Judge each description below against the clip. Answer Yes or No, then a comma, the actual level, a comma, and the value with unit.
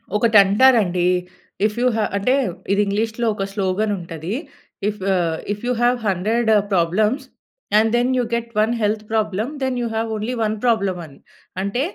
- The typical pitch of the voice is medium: No, high, 215 Hz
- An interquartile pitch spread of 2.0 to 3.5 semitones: Yes, average, 3.2 semitones